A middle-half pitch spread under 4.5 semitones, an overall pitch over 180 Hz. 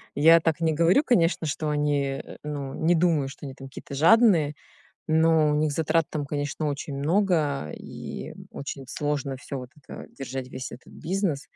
No: average, 2.9 semitones; medium, 150 Hz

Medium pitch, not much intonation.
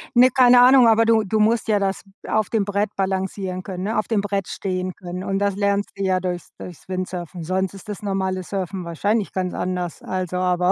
No: high, 195 Hz; narrow, 2.3 semitones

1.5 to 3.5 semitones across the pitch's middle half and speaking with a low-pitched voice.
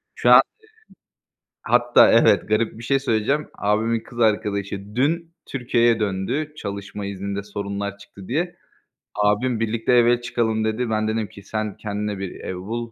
Yes: average, 2.9 semitones; low, 110 Hz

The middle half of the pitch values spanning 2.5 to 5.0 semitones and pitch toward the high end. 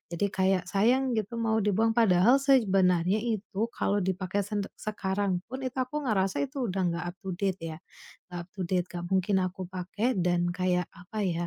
Yes: average, 3.5 semitones; high, 195 Hz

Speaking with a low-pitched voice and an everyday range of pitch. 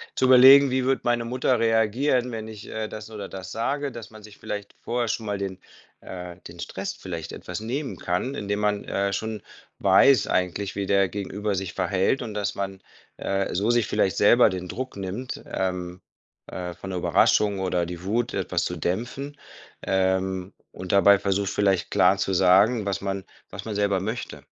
Yes: low, 100 Hz; average, 3.3 semitones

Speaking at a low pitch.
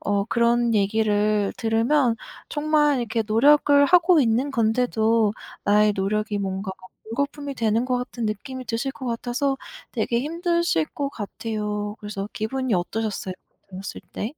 No: high, 230 Hz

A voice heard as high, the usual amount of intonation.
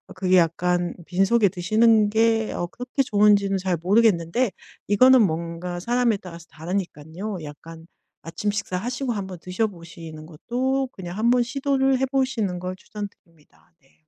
Yes: high, 195 Hz; average, 5.0 semitones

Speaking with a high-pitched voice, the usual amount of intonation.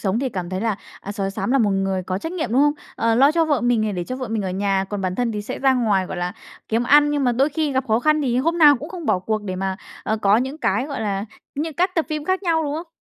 No: high, 240 Hz; wide, 6.8 semitones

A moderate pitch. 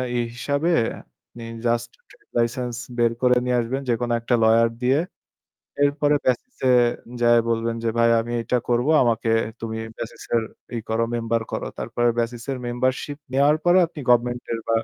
No: low, 120 Hz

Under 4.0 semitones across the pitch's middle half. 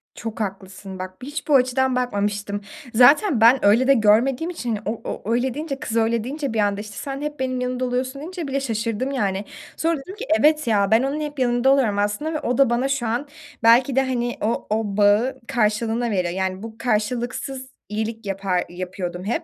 No: average, 4.3 semitones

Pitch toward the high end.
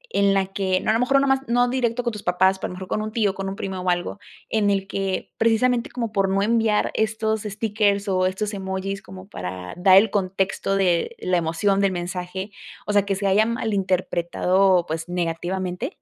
Yes: high, 195 Hz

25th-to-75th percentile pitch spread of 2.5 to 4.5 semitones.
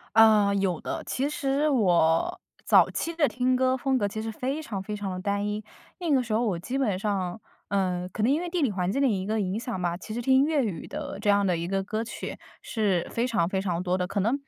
No: average, 5.2 semitones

